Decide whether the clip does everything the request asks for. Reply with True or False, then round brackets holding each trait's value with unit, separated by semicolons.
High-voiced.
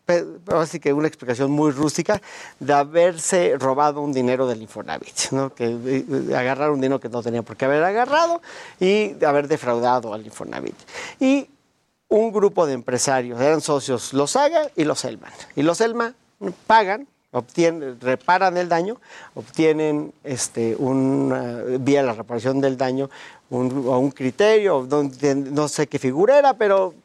False (145 Hz)